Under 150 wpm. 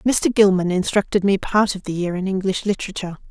No: average, 200 wpm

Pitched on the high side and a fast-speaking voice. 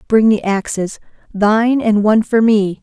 No: high, 215 Hz; average, 170 wpm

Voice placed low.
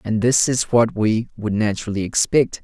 Yes: low, 110 Hz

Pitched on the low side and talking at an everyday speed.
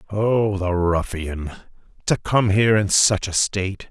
Yes: low, 100 Hz; average, 155 wpm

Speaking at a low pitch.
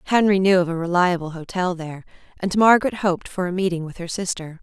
No: medium, 180 Hz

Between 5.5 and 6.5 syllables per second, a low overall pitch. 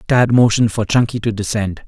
Yes: 6.0 syllables/s; low, 110 Hz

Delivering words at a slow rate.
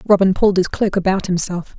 No: average, 200 wpm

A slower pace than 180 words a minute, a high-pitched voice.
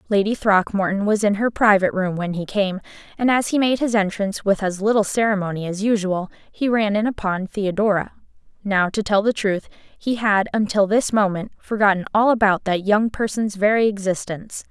No: average, 185 wpm; high, 205 Hz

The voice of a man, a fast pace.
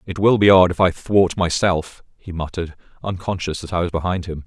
Yes: male; fast, 215 wpm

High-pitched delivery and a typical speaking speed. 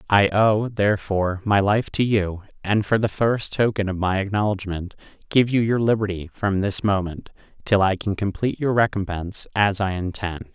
No: low, 100 Hz; average, 175 wpm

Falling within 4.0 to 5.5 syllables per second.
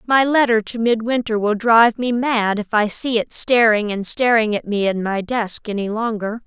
Yes: 4.8 syllables/s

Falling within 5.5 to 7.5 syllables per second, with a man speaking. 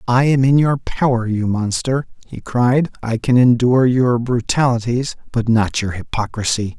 No: 4.6 syllables/s; male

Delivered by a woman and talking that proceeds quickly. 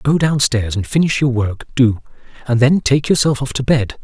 No: male; fast, 225 wpm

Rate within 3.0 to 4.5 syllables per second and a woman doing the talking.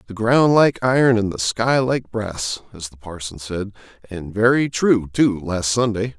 No: 4.2 syllables/s; male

